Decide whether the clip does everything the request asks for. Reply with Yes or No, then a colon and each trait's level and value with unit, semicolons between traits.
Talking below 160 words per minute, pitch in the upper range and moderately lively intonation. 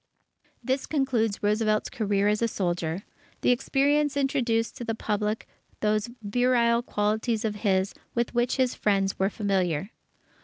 Yes: average, 140 wpm; high, 220 Hz; average, 3.0 semitones